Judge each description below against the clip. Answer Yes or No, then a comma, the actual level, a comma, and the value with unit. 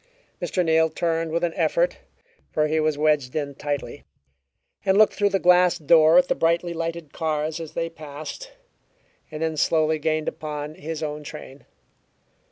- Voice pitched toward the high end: No, medium, 160 Hz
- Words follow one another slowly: No, average, 165 wpm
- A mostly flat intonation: Yes, narrow, 1.8 semitones